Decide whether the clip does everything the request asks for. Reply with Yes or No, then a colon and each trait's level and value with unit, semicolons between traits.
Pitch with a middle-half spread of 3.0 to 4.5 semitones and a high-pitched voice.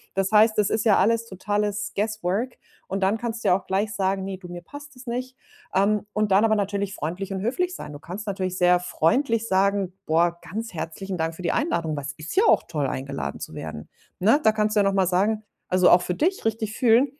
Yes: average, 3.5 semitones; high, 200 Hz